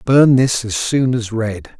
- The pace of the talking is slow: No, average, 200 wpm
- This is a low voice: Yes, low, 120 Hz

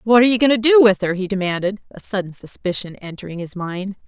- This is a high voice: Yes, high, 200 Hz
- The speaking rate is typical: No, fast, 235 wpm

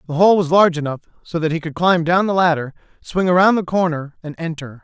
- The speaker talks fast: Yes, fast, 235 wpm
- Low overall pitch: No, medium, 170 Hz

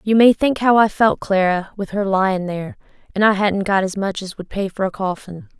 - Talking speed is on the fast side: Yes, fast, 245 wpm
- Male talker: No, female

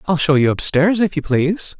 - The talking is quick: Yes, fast, 270 wpm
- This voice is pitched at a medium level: Yes, medium, 165 Hz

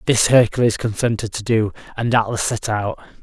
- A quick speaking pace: No, average, 170 wpm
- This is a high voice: No, low, 110 Hz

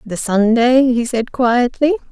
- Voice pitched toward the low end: No, high, 245 Hz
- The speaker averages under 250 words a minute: Yes, average, 140 wpm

